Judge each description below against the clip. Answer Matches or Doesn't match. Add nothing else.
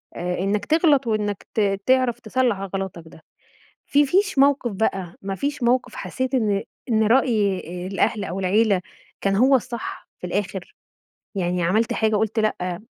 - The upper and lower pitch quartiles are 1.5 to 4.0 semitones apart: Doesn't match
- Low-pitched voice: Doesn't match